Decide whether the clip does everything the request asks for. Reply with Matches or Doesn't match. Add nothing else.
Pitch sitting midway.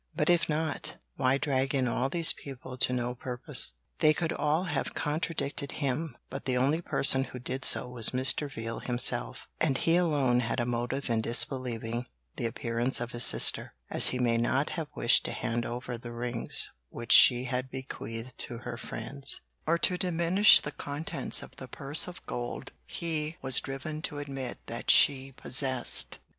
Doesn't match